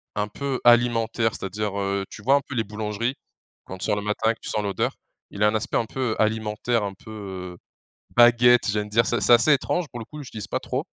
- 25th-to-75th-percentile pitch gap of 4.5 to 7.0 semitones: No, narrow, 2.5 semitones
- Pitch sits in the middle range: No, low, 110 Hz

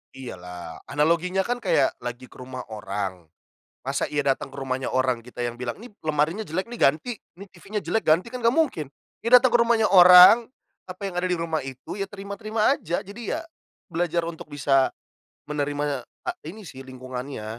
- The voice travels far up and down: Yes, wide, 7.5 semitones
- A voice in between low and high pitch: Yes, medium, 155 Hz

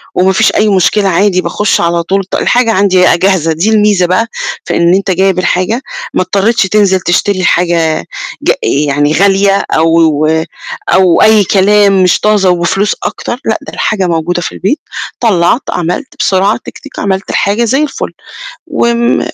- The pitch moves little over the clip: No, average, 3.2 semitones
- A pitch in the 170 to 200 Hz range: Yes, high, 190 Hz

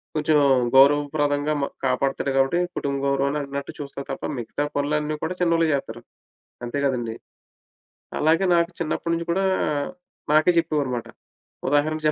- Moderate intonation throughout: No, narrow, 2.2 semitones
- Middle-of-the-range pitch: Yes, medium, 145 Hz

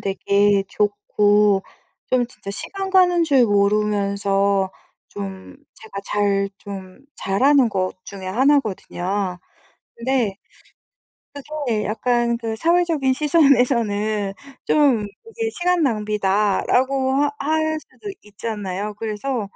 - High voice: Yes, high, 215 Hz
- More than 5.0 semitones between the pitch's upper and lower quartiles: Yes, wide, 5.4 semitones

